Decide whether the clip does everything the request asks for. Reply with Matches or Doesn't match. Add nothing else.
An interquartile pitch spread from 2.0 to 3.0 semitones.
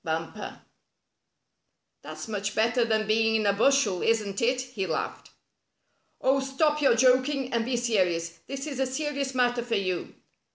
Doesn't match